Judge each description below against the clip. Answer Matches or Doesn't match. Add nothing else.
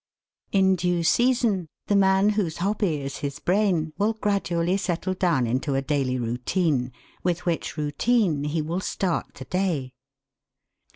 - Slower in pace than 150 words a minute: Matches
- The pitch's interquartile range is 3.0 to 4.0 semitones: Doesn't match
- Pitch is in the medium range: Matches